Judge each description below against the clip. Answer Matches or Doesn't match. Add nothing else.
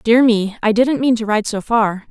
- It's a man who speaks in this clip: Doesn't match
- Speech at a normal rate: Doesn't match